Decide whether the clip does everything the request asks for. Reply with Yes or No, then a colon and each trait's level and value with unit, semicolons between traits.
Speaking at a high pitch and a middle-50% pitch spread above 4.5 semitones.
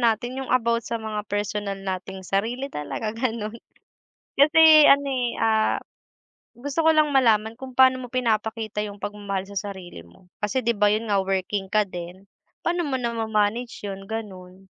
No: high, 220 Hz; average, 3.8 semitones